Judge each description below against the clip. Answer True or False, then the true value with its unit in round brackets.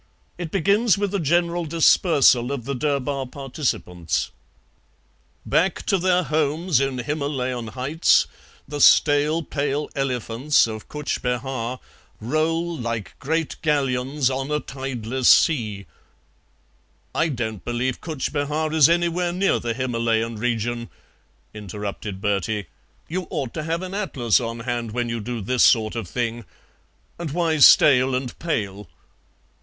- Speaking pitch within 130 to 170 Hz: True (135 Hz)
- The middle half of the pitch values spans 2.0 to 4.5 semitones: False (5.1 semitones)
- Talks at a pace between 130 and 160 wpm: True (135 wpm)